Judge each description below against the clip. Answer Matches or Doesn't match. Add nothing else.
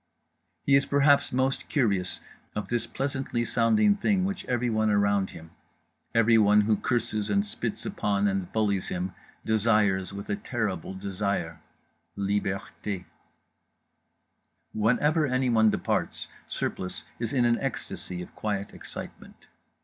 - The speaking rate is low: Matches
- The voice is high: Doesn't match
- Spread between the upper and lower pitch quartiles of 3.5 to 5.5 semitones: Matches